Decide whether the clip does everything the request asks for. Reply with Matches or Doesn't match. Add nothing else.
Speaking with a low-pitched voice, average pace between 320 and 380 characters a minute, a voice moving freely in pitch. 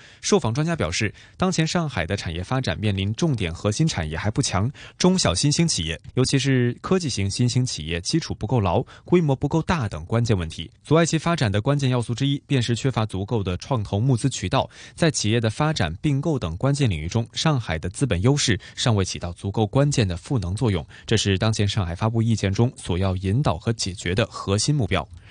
Matches